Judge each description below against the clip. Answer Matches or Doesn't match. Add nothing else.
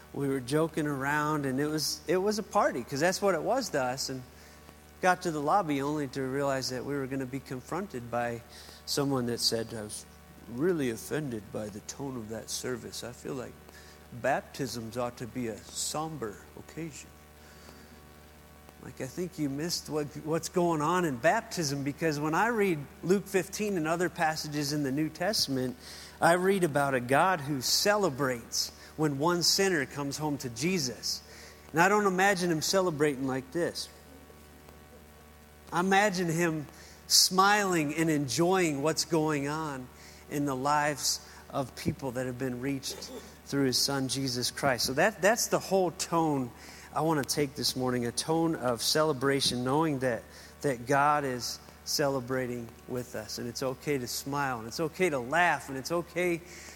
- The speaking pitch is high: Doesn't match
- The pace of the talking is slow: Doesn't match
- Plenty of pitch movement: Matches